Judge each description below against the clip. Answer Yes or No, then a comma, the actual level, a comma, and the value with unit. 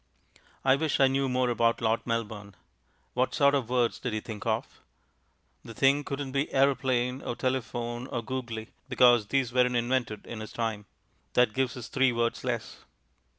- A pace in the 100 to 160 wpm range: No, average, 170 wpm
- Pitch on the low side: Yes, low, 125 Hz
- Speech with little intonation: Yes, narrow, 2.3 semitones